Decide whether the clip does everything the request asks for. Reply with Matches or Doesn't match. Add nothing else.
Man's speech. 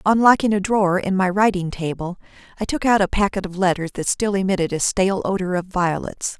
Doesn't match